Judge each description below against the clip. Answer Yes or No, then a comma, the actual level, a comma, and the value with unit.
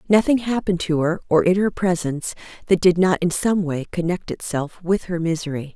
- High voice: No, medium, 175 Hz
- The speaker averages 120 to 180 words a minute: No, average, 200 wpm